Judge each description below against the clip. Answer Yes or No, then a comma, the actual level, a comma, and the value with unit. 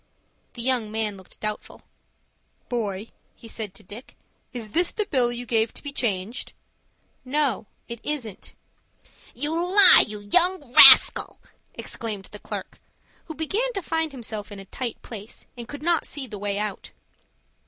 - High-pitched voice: Yes, high, 235 Hz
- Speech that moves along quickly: No, average, 155 wpm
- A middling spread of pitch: No, wide, 5.8 semitones